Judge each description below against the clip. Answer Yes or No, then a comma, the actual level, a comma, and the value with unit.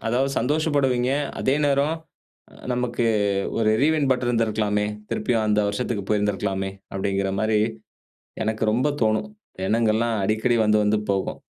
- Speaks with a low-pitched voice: Yes, low, 110 Hz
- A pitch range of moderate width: Yes, average, 3.2 semitones